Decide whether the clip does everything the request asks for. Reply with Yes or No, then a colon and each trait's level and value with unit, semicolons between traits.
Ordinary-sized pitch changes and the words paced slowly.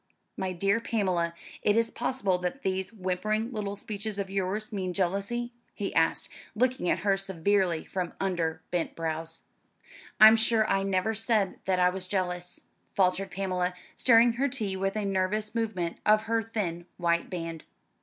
No: average, 3.1 semitones; average, 160 wpm